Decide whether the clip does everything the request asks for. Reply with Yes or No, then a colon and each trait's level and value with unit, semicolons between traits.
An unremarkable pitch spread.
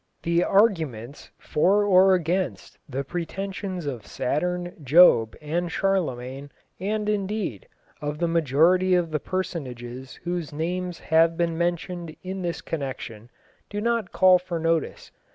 Yes: average, 3.9 semitones